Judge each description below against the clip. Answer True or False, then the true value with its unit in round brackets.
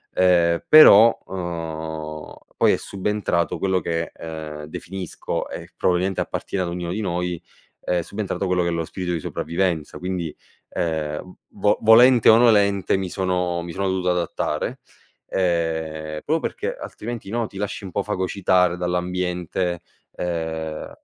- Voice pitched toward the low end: True (90 Hz)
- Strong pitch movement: False (2.6 semitones)